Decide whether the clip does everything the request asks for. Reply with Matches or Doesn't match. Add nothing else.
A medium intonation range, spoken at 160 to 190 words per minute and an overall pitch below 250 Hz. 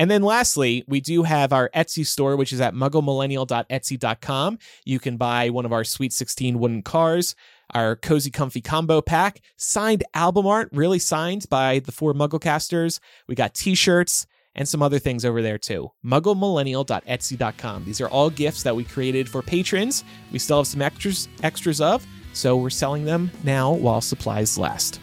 Matches